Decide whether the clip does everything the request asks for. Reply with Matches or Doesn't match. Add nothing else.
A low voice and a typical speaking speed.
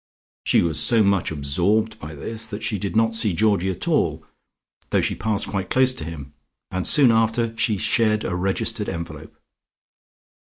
Matches